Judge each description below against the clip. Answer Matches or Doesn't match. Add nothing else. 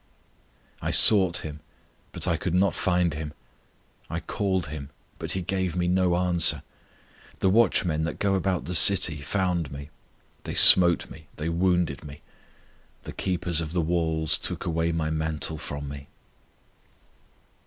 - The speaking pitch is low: Matches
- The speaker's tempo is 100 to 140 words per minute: Doesn't match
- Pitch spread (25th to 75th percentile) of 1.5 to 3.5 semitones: Matches